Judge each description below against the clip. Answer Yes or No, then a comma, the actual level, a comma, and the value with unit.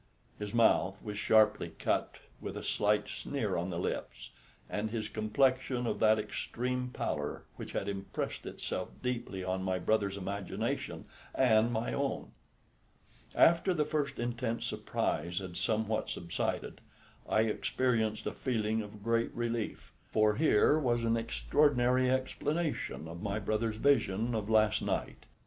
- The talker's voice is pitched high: No, low, 110 Hz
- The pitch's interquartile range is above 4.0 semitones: No, average, 3.3 semitones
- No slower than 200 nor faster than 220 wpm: No, average, 140 wpm